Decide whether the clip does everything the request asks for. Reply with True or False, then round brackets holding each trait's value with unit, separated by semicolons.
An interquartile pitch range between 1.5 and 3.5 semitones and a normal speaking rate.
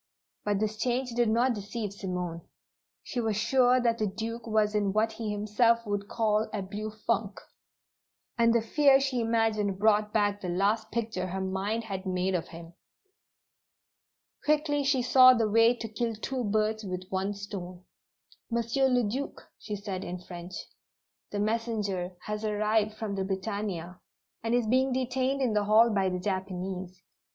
True (3.0 semitones; 165 wpm)